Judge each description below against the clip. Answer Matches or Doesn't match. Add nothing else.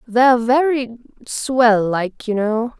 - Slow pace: Matches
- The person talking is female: Matches